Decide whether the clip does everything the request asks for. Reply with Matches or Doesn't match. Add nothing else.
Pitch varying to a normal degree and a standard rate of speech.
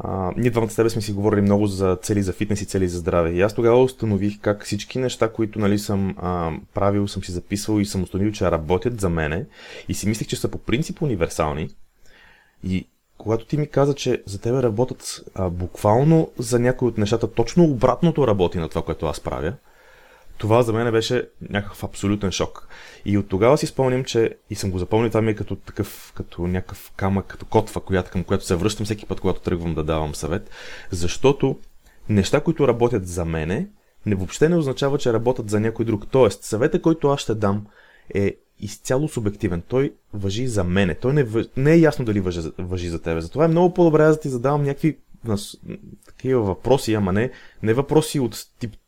Doesn't match